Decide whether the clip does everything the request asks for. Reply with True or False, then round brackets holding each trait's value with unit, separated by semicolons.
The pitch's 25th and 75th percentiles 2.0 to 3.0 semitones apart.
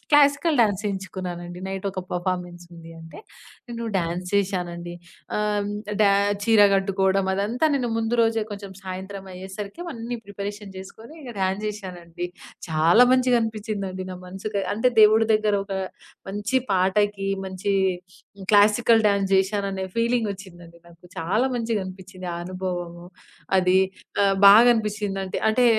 True (2.7 semitones)